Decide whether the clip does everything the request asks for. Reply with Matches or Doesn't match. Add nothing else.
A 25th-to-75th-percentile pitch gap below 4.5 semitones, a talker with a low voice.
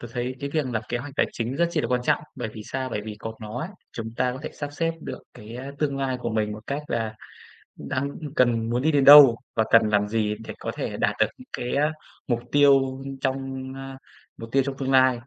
Matches